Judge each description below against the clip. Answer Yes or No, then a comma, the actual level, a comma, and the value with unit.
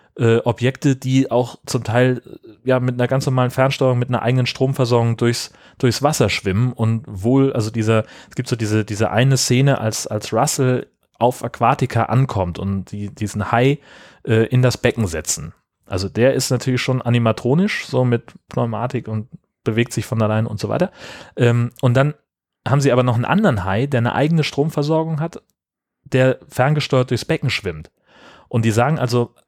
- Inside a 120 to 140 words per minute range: No, average, 175 wpm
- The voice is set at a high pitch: No, low, 125 Hz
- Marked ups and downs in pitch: No, average, 2.8 semitones